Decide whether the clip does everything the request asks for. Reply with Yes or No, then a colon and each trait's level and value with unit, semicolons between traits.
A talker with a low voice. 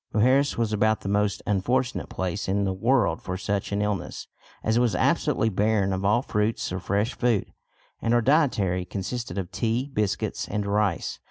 Yes: low, 105 Hz